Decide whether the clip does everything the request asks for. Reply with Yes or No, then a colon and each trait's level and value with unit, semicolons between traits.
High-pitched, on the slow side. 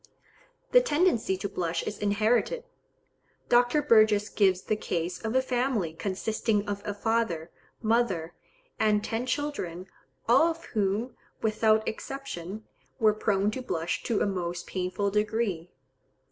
Yes: high, 215 Hz; slow, 130 wpm